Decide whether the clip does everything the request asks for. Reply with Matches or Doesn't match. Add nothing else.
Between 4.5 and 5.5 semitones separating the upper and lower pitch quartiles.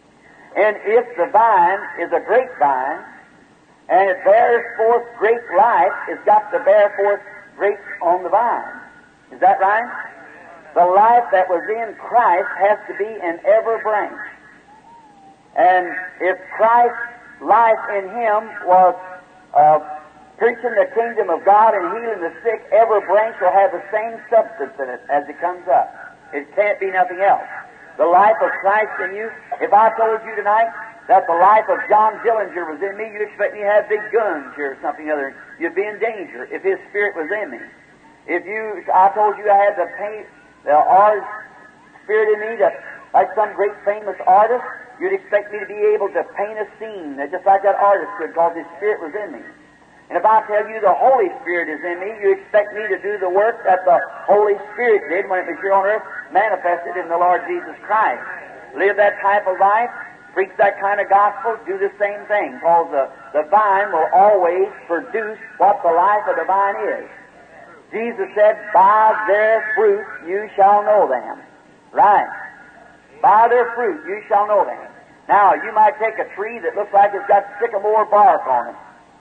Doesn't match